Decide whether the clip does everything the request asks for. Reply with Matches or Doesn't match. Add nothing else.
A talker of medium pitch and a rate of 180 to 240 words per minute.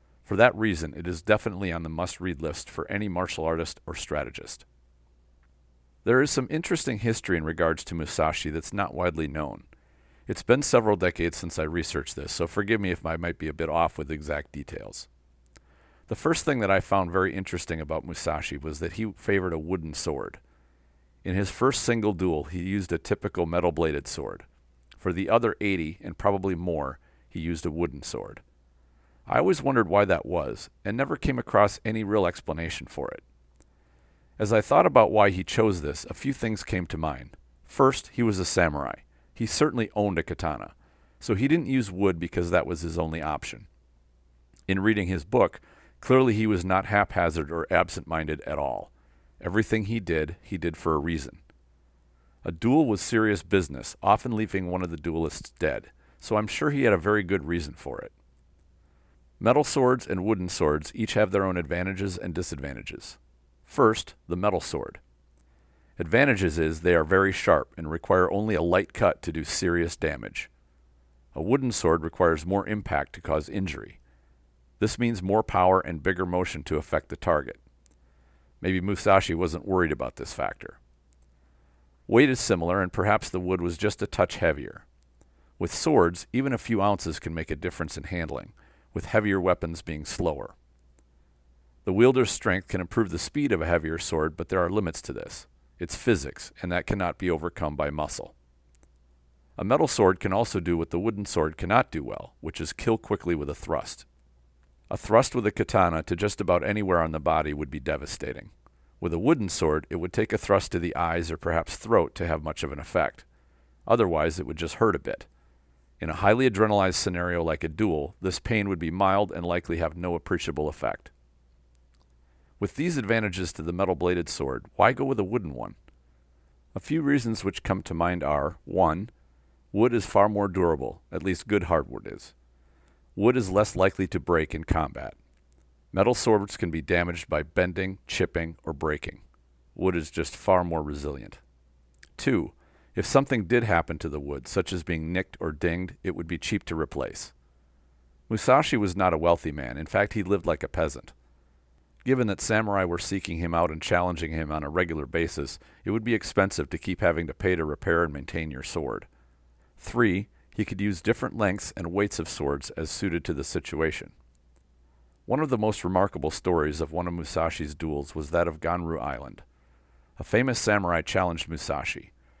Doesn't match